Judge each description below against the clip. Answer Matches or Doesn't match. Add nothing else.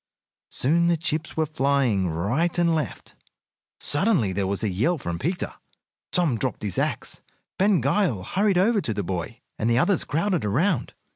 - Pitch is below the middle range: Doesn't match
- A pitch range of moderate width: Doesn't match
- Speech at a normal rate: Matches